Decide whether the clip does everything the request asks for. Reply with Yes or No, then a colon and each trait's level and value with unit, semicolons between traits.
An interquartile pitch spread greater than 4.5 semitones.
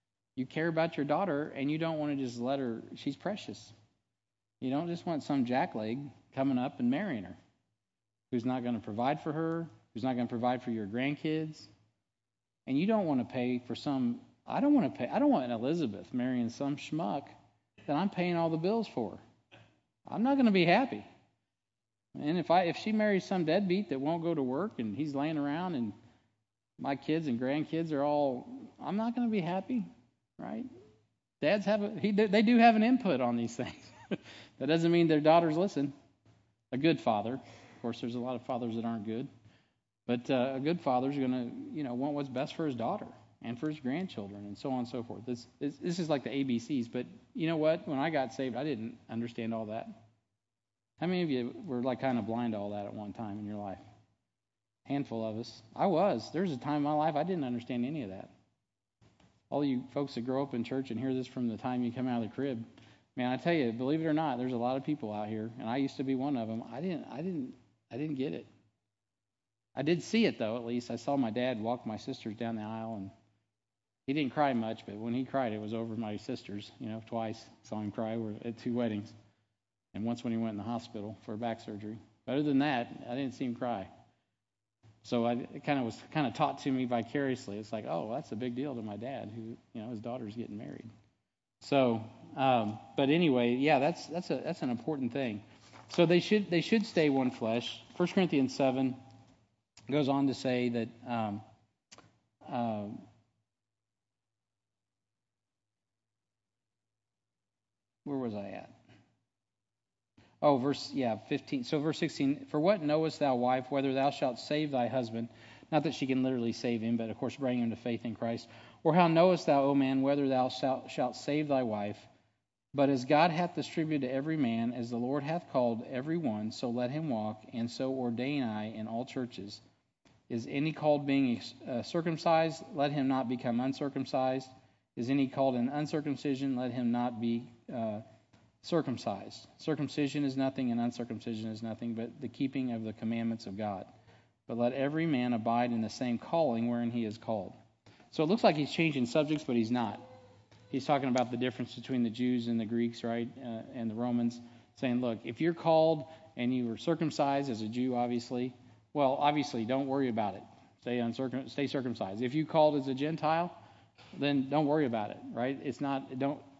No: average, 4.1 semitones